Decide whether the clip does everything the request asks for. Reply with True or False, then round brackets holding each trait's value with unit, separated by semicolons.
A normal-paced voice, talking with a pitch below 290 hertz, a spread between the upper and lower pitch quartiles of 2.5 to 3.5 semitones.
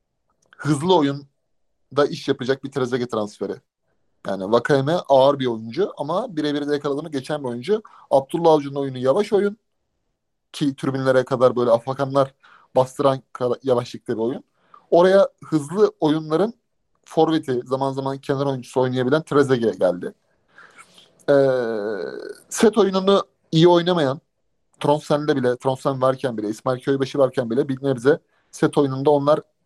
True (125 wpm; 140 Hz; 3.2 semitones)